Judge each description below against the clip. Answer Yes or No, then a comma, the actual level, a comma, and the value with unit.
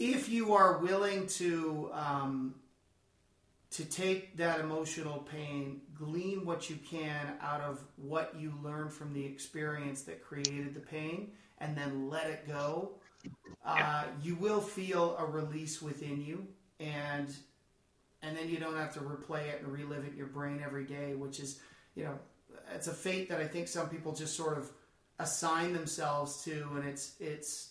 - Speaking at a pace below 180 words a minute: Yes, average, 170 wpm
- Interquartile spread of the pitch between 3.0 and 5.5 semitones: No, narrow, 2.5 semitones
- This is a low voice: No, medium, 150 Hz